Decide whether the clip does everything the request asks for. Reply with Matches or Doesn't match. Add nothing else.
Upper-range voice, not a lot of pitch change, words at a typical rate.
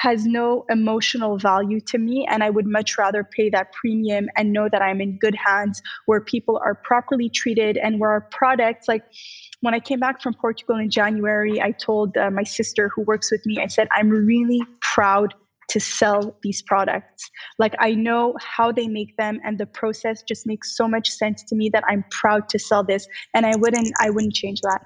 Doesn't match